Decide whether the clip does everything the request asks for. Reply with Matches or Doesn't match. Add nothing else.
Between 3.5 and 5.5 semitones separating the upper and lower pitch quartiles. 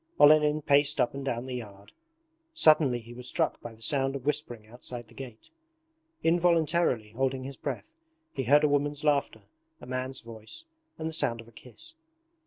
Matches